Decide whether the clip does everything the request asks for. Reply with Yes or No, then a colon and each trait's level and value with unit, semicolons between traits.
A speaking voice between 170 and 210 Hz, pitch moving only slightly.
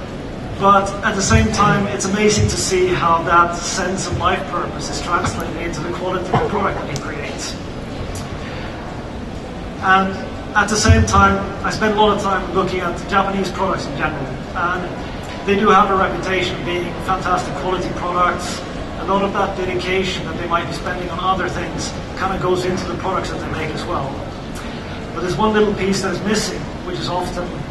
Yes: medium, 185 Hz; narrow, 1.8 semitones